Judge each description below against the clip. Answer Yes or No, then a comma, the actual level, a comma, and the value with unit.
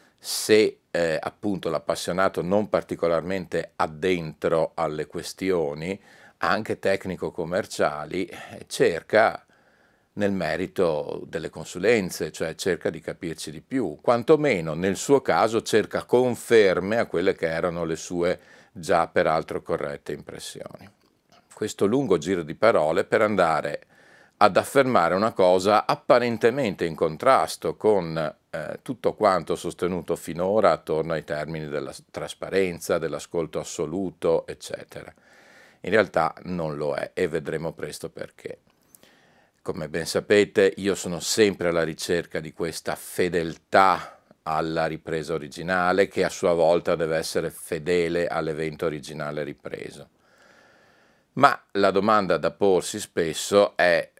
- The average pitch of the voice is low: Yes, low, 100 Hz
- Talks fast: No, slow, 115 wpm